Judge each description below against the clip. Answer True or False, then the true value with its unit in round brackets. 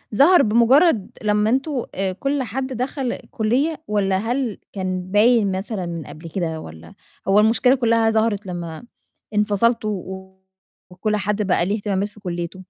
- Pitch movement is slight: False (4.0 semitones)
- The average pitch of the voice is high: True (210 Hz)